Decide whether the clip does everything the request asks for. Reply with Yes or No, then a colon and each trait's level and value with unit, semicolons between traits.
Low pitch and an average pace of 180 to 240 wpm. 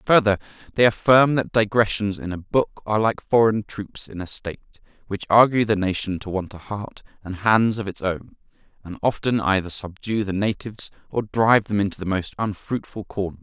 Yes: low, 105 Hz; average, 190 wpm